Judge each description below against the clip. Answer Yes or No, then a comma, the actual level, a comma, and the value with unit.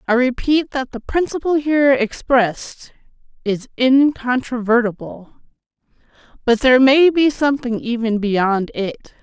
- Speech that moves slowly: Yes, slow, 110 wpm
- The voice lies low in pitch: No, very high, 250 Hz